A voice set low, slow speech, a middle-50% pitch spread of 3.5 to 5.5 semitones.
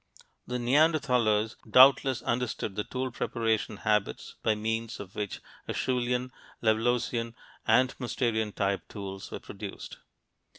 No: low, 115 Hz; slow, 115 wpm; average, 2.7 semitones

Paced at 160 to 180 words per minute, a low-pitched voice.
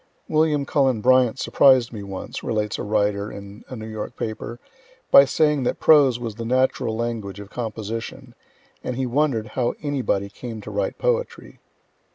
Yes: average, 165 wpm; low, 120 Hz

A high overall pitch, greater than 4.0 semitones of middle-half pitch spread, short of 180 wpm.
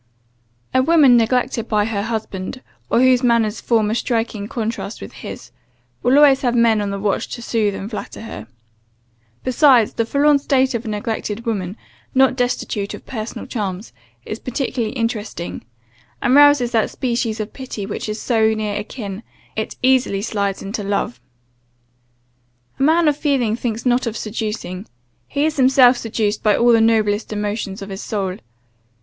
No: high, 225 Hz; average, 3.3 semitones; average, 165 wpm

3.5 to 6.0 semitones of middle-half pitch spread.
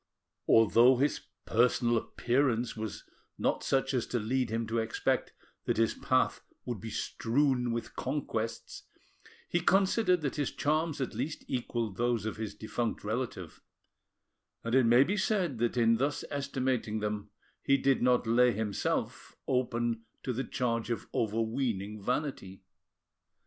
No: average, 3.0 semitones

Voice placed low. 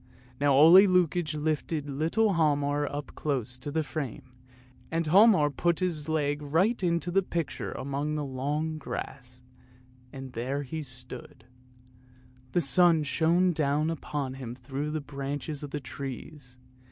No: medium, 150 Hz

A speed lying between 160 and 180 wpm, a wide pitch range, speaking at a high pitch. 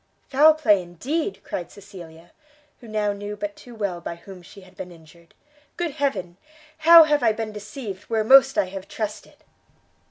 Yes: average, 170 wpm; wide, 6.5 semitones; high, 210 Hz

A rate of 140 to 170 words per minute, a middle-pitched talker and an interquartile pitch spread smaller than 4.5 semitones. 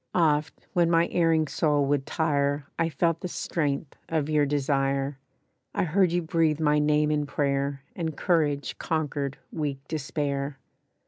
Yes: average, 145 wpm; medium, 150 Hz; narrow, 2.5 semitones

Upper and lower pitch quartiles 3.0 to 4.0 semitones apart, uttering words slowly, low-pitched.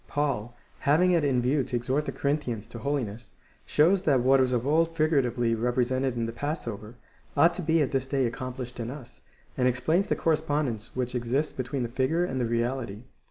No: average, 3.7 semitones; average, 200 wpm; low, 130 Hz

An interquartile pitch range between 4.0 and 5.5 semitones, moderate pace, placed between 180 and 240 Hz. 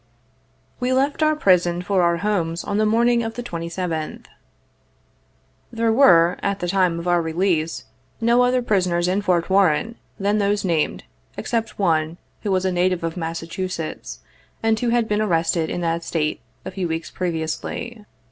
Yes: average, 4.3 semitones; average, 165 wpm; medium, 185 Hz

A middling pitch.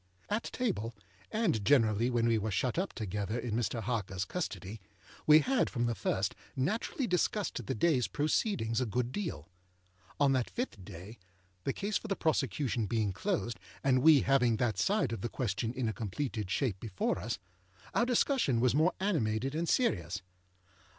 No: low, 120 Hz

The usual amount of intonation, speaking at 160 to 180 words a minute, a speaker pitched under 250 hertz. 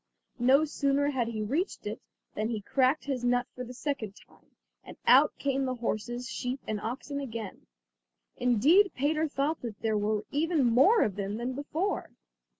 No: average, 3.9 semitones; average, 170 wpm; very high, 255 Hz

